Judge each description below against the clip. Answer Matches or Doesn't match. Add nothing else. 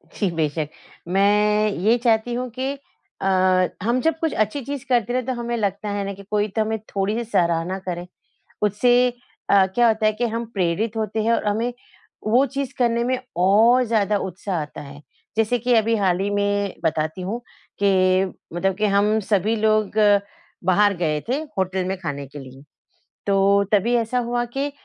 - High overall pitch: Matches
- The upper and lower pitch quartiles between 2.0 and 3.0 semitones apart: Doesn't match